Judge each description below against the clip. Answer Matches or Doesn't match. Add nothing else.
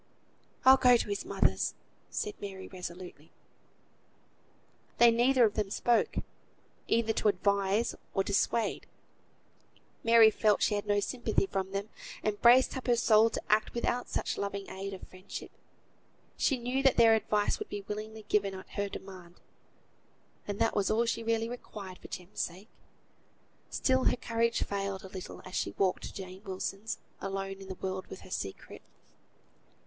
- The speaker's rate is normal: Matches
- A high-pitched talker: Matches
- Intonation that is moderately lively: Matches